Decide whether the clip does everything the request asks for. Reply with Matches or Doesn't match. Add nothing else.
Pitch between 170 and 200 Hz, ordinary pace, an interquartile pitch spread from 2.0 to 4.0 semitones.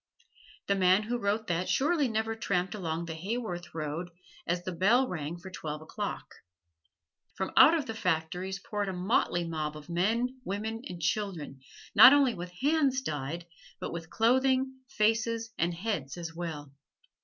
Doesn't match